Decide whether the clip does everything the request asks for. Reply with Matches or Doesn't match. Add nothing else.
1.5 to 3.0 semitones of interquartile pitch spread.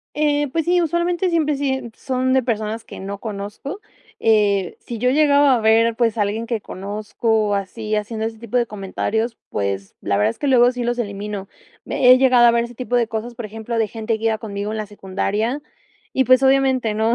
Doesn't match